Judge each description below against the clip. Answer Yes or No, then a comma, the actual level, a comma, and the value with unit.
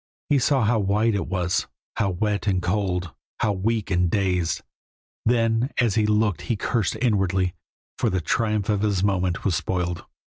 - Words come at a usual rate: Yes, average, 170 wpm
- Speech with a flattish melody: No, average, 3.2 semitones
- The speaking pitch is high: No, low, 100 Hz